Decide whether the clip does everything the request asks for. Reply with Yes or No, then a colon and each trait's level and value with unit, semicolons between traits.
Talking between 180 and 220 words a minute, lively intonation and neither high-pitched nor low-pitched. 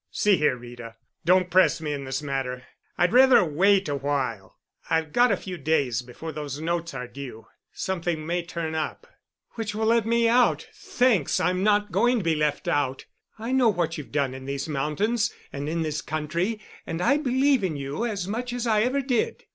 Yes: average, 195 wpm; wide, 7.0 semitones; medium, 170 Hz